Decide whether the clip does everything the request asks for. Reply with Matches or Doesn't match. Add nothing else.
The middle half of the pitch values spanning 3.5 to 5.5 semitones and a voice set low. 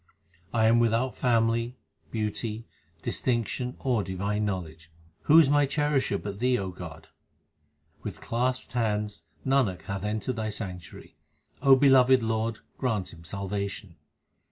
Matches